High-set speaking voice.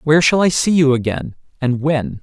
No: medium, 145 Hz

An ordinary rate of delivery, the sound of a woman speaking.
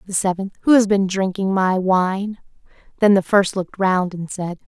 Yes: average, 190 wpm; female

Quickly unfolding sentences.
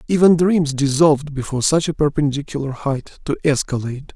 No: average, 145 wpm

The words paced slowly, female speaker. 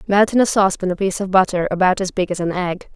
No: fast, 285 wpm; female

